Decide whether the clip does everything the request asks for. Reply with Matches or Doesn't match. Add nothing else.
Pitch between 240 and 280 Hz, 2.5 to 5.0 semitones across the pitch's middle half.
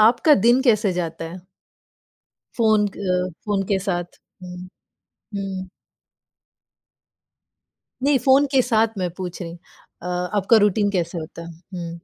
Doesn't match